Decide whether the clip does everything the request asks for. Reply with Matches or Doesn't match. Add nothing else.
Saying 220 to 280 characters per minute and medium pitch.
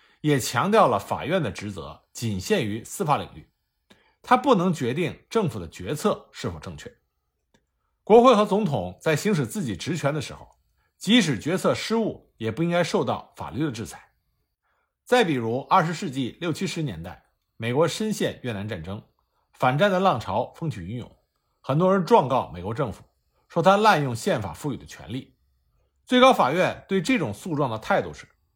Matches